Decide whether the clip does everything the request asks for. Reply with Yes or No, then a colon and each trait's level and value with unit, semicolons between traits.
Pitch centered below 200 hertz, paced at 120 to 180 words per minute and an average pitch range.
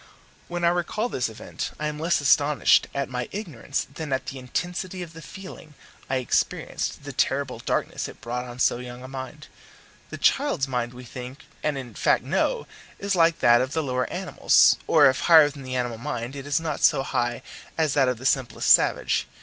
No: low, 135 Hz; average, 200 wpm; average, 4.2 semitones